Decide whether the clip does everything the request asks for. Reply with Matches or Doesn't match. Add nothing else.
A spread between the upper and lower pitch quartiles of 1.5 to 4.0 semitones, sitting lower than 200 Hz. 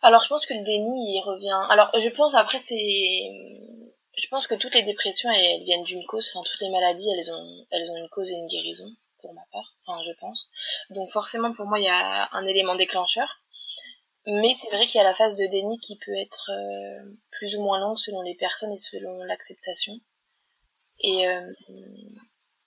Doesn't match